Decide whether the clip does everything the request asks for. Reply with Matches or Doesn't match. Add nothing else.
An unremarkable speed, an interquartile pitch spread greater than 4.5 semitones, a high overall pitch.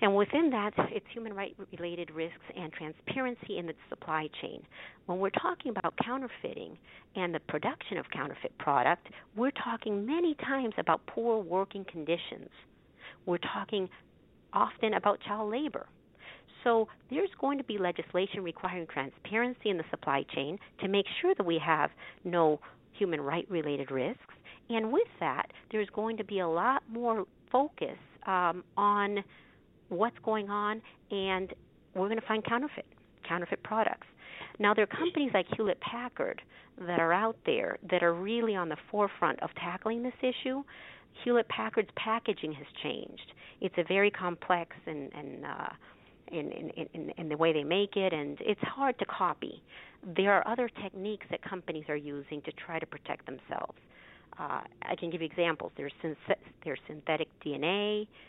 Matches